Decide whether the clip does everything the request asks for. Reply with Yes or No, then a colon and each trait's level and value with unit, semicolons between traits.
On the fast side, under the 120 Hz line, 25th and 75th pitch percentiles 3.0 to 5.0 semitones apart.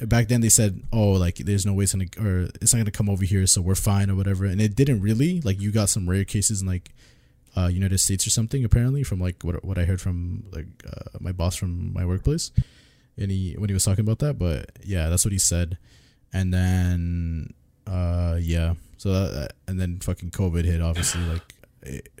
Yes: fast, 225 wpm; very low, 95 Hz; average, 3.3 semitones